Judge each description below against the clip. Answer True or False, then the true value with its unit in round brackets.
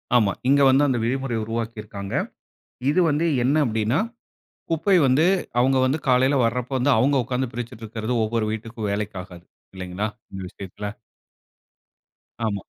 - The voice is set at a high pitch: False (115 Hz)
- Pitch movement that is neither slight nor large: True (3.7 semitones)